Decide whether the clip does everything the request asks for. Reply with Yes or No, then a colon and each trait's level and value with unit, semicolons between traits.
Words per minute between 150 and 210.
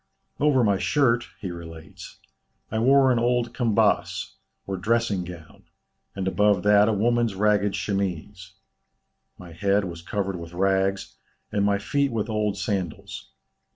No: average, 140 wpm